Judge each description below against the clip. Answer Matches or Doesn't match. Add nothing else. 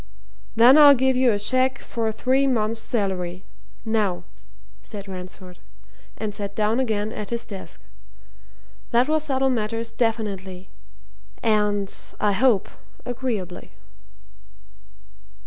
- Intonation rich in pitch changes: Doesn't match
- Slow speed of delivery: Matches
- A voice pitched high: Matches